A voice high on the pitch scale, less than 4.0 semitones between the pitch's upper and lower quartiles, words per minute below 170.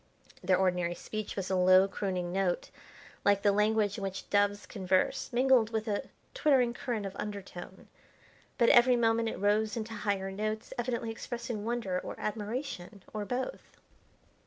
Yes: high, 210 Hz; average, 3.1 semitones; average, 155 wpm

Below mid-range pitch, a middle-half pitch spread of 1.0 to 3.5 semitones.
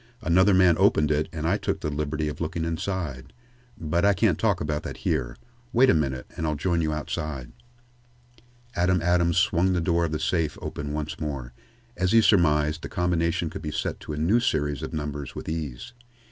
Yes: very low, 80 Hz; average, 2.9 semitones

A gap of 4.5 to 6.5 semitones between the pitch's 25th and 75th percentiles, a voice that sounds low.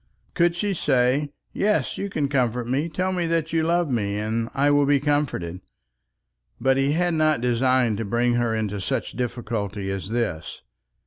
Yes: average, 5.3 semitones; low, 130 Hz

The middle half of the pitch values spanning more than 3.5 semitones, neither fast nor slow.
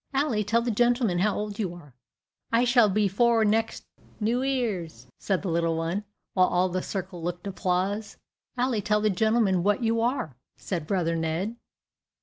Yes: average, 4.3 semitones; average, 170 wpm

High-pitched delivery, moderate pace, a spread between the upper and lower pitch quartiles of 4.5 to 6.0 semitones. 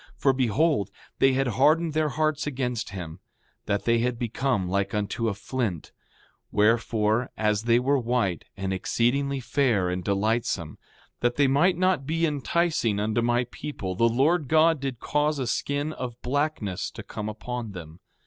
No: low, 120 Hz; average, 160 wpm; average, 5.3 semitones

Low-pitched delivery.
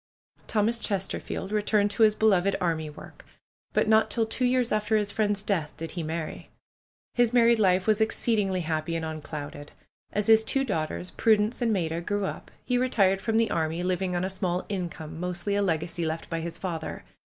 No: high, 195 Hz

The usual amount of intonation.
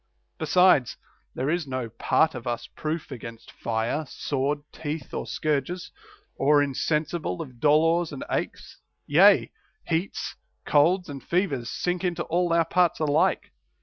Yes: average, 4.1 semitones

